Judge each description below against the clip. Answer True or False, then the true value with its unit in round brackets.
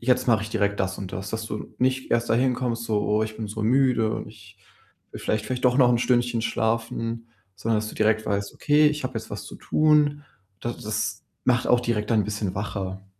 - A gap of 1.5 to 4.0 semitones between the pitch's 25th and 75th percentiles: True (2.7 semitones)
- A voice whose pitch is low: True (115 Hz)